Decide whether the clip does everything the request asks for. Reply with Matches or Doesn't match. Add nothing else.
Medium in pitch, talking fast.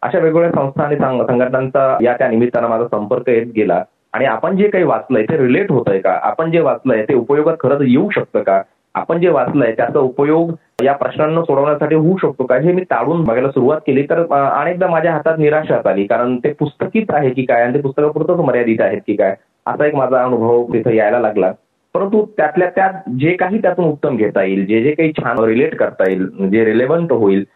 Matches